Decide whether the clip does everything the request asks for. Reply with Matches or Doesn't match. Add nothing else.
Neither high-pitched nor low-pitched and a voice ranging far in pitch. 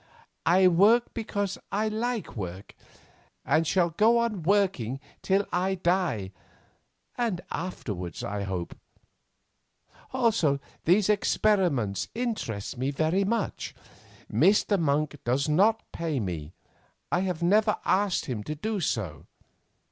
Matches